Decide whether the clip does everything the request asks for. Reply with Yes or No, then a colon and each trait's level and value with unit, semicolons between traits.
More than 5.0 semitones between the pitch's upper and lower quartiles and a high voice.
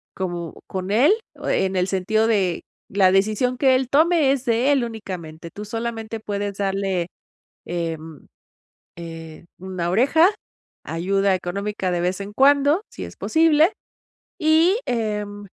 Yes: wide, 5.5 semitones; high, 205 Hz